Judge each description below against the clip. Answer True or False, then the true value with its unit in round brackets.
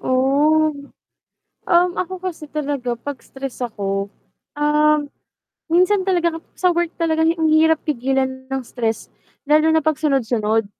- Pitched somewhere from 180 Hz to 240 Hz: False (300 Hz)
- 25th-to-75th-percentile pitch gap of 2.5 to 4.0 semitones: True (3.7 semitones)